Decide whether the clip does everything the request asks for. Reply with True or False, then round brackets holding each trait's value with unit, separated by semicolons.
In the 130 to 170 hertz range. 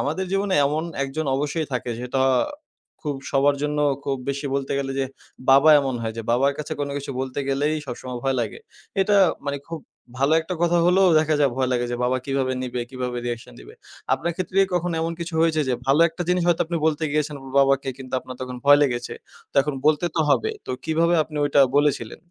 True (140 Hz)